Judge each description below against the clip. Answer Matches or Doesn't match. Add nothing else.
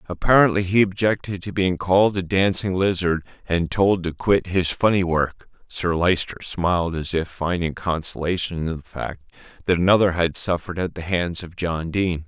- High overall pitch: Doesn't match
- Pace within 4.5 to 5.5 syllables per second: Matches